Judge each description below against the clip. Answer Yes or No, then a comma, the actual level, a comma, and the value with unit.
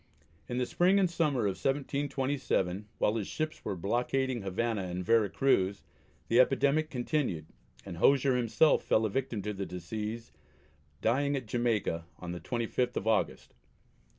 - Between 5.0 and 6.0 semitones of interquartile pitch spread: Yes, wide, 5.4 semitones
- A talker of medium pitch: No, low, 120 Hz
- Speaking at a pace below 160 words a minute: Yes, average, 150 wpm